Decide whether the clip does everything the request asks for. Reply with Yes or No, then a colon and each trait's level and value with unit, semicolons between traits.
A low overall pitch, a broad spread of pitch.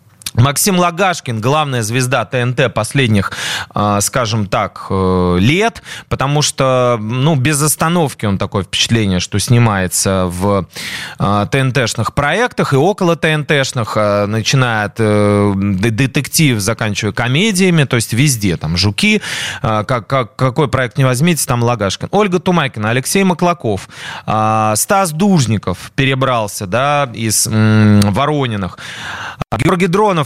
Yes: low, 125 Hz; wide, 6.0 semitones